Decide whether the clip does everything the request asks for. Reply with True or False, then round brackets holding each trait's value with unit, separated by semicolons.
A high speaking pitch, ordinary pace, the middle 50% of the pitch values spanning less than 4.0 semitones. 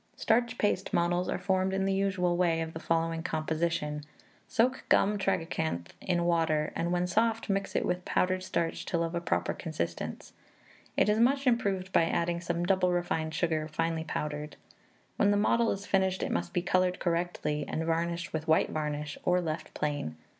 False (175 Hz; 180 wpm; 2.8 semitones)